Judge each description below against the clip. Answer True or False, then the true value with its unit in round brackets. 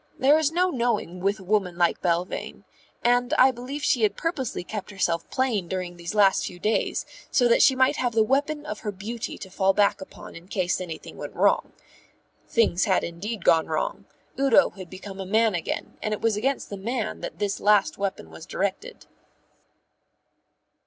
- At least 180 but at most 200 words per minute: True (185 wpm)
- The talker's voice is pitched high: True (210 Hz)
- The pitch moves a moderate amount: True (4.8 semitones)